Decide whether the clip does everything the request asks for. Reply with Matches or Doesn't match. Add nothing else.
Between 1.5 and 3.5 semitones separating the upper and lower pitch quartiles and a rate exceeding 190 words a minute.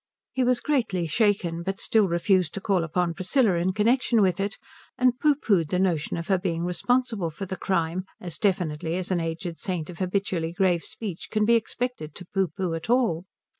Doesn't match